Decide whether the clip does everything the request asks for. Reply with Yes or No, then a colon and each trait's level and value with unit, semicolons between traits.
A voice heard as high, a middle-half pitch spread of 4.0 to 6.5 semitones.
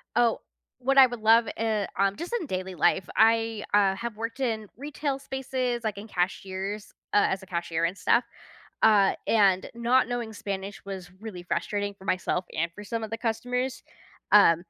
No: high, 215 Hz; average, 3.5 semitones